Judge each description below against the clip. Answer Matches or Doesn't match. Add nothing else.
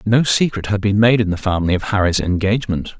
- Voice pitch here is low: Matches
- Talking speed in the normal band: Doesn't match